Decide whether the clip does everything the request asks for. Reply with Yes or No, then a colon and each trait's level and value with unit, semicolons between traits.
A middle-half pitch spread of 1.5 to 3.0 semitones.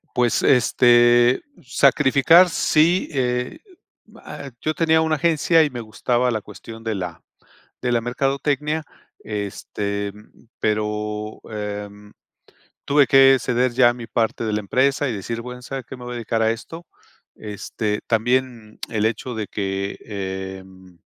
No: average, 4.0 semitones